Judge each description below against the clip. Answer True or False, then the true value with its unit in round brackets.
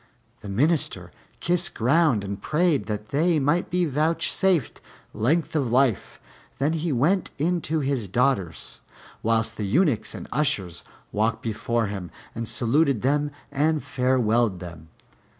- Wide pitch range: True (6.4 semitones)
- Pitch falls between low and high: False (130 Hz)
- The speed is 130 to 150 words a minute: True (135 wpm)